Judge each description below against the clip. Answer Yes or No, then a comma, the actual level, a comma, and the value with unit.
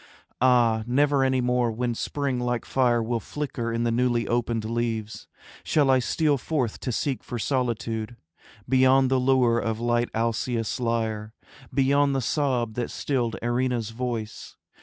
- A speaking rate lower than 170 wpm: Yes, average, 150 wpm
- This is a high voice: No, low, 120 Hz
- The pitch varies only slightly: Yes, narrow, 2.1 semitones